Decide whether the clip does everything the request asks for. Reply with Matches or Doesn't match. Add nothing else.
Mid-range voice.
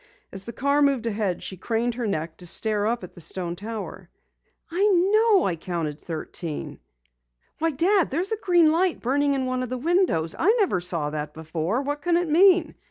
Doesn't match